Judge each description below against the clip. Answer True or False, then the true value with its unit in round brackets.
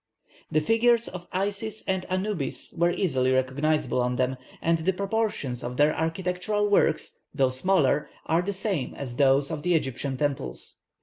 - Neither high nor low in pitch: True (160 Hz)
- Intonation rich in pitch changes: True (6.2 semitones)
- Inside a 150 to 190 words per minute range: True (160 wpm)